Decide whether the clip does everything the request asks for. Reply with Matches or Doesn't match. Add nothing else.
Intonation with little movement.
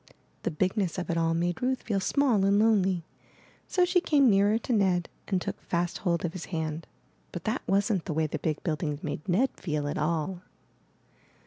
Doesn't match